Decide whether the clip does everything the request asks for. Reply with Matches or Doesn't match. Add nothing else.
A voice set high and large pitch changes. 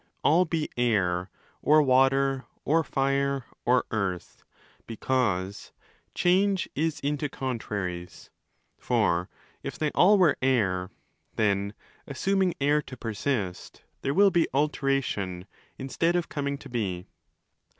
Doesn't match